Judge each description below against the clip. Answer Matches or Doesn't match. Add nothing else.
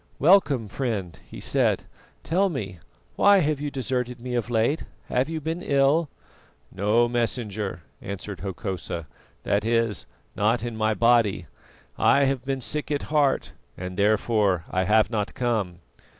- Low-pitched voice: Matches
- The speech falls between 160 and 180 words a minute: Doesn't match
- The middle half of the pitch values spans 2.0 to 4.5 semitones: Doesn't match